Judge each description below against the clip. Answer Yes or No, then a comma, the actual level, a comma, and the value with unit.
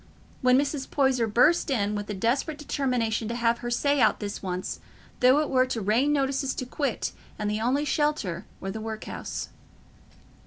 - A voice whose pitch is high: Yes, very high, 250 Hz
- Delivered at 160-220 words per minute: Yes, average, 185 wpm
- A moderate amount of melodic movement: Yes, average, 4.3 semitones